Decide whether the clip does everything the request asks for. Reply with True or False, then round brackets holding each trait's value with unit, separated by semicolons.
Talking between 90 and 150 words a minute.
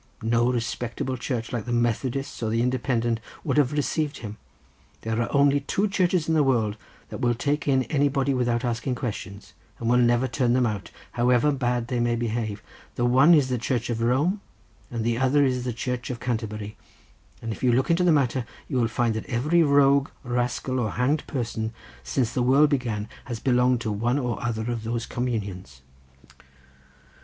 False (185 wpm)